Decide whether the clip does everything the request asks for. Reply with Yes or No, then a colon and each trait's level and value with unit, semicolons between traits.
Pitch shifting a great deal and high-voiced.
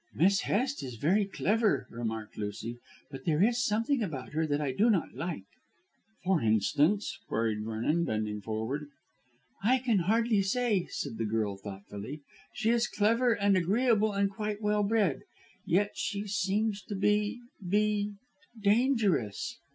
Yes: wide, 8.7 semitones; high, 195 Hz